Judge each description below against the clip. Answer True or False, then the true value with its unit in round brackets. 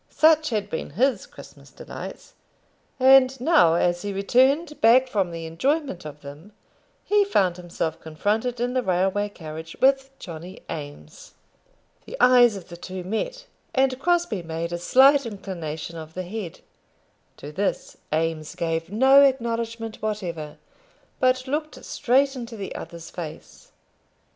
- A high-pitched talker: True (205 Hz)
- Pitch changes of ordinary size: False (7.5 semitones)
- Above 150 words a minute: False (140 wpm)